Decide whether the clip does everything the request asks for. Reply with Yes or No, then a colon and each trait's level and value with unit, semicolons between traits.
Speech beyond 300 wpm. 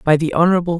No: fast, 225 wpm